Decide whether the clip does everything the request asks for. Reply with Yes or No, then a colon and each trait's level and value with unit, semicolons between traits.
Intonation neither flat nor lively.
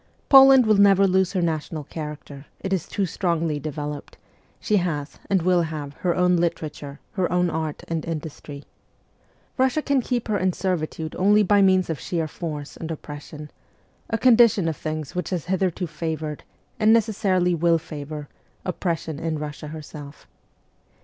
Yes: average, 3.7 semitones